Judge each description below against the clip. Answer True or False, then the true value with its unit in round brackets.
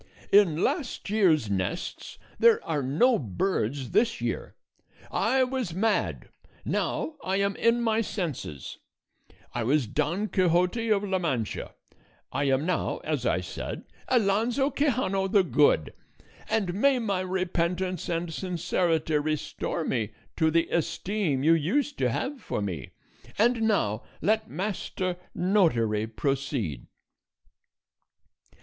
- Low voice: False (180 Hz)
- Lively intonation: True (6.7 semitones)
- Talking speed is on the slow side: True (125 wpm)